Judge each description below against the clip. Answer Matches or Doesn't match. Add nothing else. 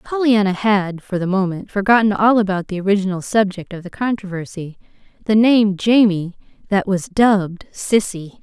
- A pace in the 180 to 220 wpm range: Doesn't match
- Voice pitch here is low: Doesn't match